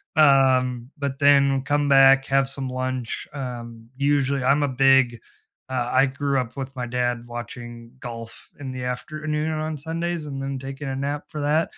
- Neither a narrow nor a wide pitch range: No, narrow, 2.3 semitones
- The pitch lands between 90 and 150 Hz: Yes, low, 135 Hz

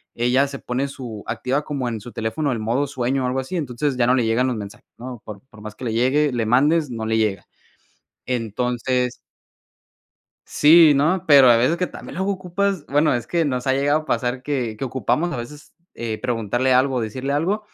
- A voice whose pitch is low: Yes, low, 130 Hz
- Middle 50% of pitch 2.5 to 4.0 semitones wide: Yes, average, 3.6 semitones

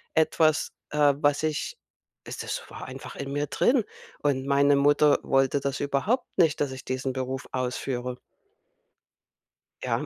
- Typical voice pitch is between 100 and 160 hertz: Yes, medium, 140 Hz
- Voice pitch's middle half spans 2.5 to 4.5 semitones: No, narrow, 2.0 semitones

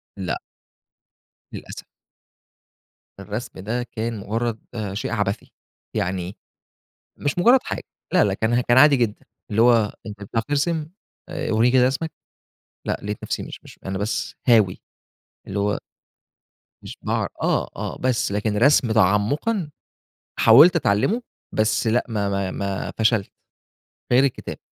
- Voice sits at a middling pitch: No, low, 110 Hz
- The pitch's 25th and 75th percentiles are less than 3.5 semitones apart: No, average, 3.8 semitones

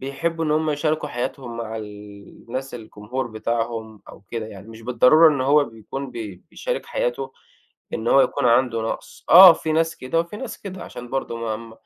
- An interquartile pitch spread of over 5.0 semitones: Yes, wide, 5.5 semitones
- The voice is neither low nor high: No, low, 125 Hz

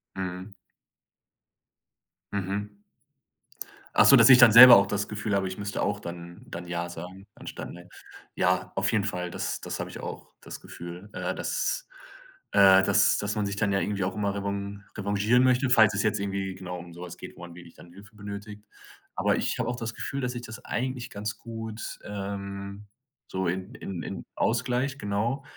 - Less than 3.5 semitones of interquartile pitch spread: Yes, narrow, 2.6 semitones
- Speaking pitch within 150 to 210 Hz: No, low, 100 Hz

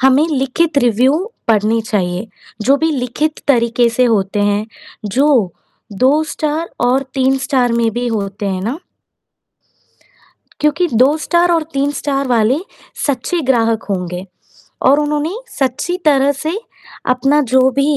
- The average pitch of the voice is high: Yes, very high, 260 Hz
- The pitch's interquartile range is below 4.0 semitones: No, average, 4.3 semitones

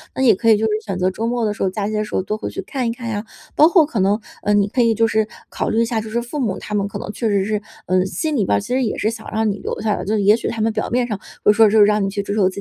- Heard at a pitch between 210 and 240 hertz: Yes, high, 215 Hz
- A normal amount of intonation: No, narrow, 2.2 semitones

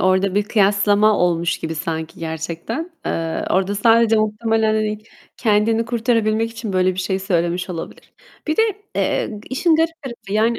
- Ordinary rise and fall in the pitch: Yes, average, 3.8 semitones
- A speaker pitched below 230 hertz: Yes, high, 210 Hz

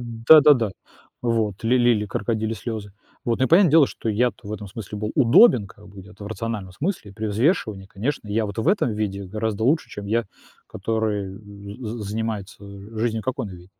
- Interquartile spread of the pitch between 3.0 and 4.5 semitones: No, narrow, 2.6 semitones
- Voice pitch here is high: No, low, 110 Hz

